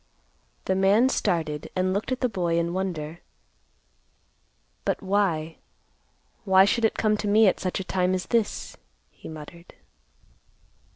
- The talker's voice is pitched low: No, high, 190 Hz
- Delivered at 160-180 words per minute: No, average, 140 wpm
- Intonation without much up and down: No, average, 3.3 semitones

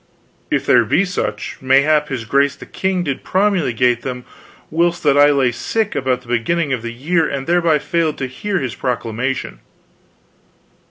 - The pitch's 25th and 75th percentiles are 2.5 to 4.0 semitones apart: No, average, 5.2 semitones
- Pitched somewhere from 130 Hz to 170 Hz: Yes, medium, 140 Hz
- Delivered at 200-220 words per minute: No, average, 165 wpm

